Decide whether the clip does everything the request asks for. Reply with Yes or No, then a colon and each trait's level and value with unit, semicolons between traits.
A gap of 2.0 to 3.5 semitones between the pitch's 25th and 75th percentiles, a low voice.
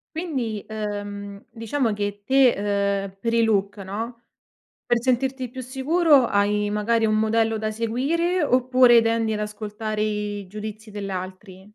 No: average, 2.9 semitones; high, 220 Hz